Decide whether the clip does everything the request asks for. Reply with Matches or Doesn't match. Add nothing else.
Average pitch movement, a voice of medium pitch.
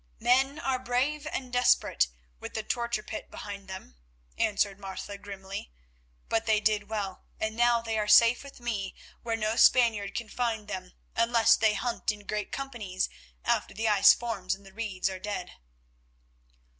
Doesn't match